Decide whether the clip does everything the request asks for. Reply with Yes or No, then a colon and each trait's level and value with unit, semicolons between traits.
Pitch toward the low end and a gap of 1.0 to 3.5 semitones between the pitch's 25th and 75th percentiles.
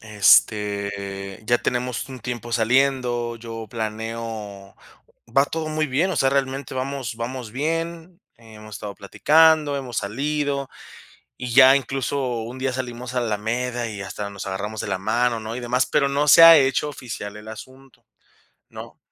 No: low, 120 Hz; average, 3.9 semitones